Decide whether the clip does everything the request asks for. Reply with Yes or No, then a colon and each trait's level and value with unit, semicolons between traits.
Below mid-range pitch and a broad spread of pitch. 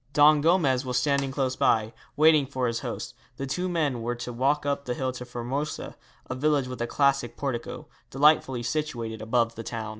No: low, 130 Hz; average, 3.3 semitones